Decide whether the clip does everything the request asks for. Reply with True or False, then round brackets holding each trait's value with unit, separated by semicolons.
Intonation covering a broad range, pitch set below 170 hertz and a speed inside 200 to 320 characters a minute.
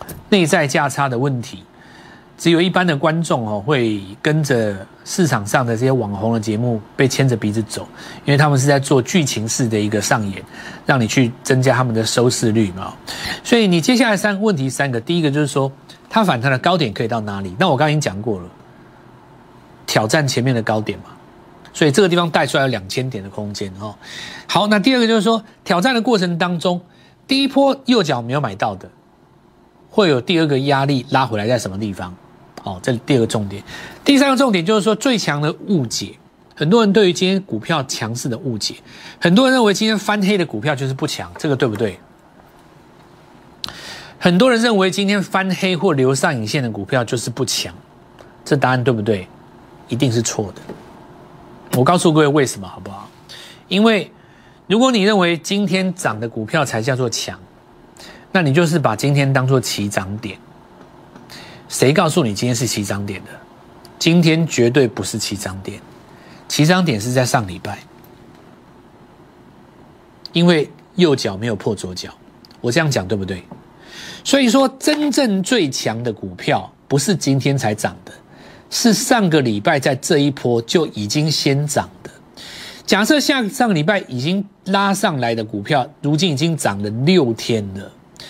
True (8.2 semitones; 140 Hz; 270 characters per minute)